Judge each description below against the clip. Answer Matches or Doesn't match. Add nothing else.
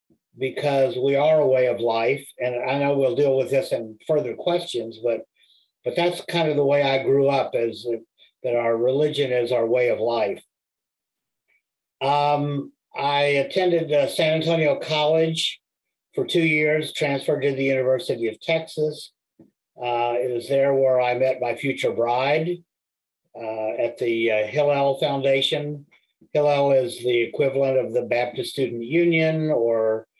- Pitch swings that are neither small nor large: Matches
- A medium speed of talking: Matches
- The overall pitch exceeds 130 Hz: Matches